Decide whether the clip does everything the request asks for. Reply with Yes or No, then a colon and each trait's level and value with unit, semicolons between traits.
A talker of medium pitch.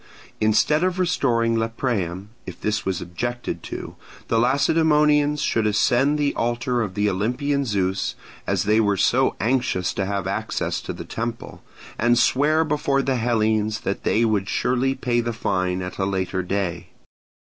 No: low, 115 Hz